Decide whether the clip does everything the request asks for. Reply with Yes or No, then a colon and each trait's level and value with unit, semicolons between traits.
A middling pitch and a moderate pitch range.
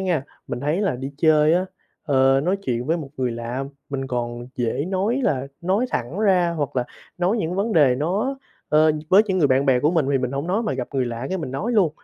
No: medium, 150 Hz; wide, 6.1 semitones